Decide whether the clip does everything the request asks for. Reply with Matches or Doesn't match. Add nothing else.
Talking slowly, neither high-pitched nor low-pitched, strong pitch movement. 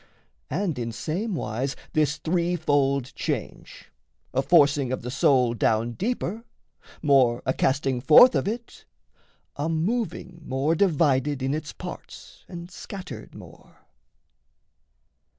Doesn't match